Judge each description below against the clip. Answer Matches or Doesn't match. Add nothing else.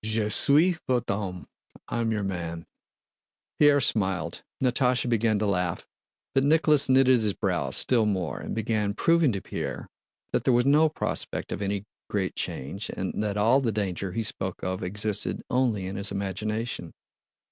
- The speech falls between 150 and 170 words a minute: Matches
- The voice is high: Doesn't match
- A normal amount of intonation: Matches